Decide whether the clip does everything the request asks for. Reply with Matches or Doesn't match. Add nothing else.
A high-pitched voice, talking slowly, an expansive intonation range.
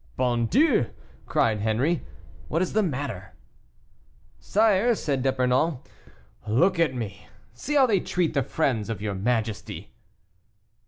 Doesn't match